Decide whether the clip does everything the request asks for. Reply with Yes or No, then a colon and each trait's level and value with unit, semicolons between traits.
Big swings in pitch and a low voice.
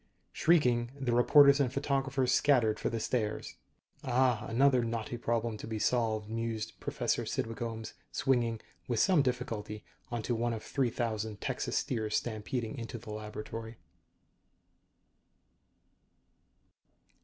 No: narrow, 2.4 semitones; low, 115 Hz